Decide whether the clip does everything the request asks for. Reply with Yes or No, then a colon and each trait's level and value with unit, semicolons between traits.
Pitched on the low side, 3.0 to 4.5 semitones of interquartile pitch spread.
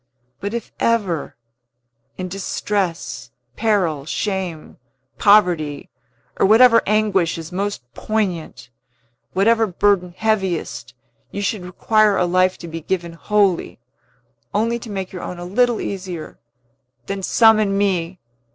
No: high, 190 Hz; average, 3.5 semitones